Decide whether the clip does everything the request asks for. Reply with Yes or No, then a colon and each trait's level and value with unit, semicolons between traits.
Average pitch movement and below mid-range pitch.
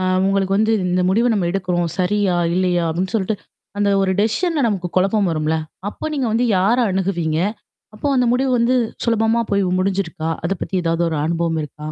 No: average, 3.8 semitones; high, 190 Hz